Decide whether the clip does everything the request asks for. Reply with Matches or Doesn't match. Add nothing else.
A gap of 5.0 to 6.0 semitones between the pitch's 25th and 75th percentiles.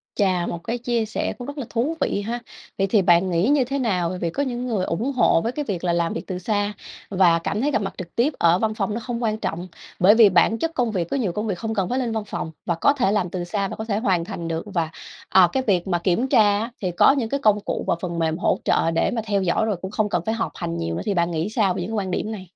Doesn't match